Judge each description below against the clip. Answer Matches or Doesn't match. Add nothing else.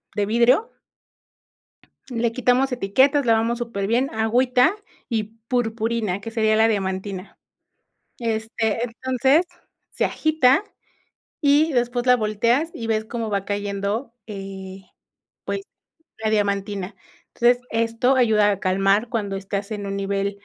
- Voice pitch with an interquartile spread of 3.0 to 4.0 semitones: Matches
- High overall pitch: Matches